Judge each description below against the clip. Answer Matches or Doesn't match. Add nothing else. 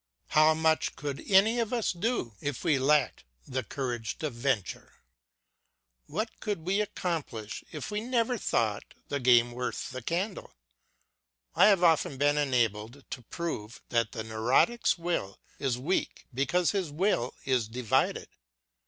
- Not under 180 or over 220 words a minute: Doesn't match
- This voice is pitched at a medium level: Matches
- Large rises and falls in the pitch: Matches